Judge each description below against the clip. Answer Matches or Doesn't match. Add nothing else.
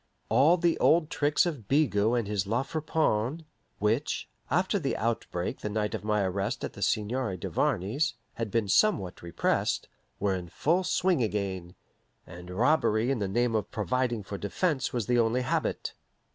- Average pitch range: Doesn't match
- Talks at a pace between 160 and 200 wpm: Matches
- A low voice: Matches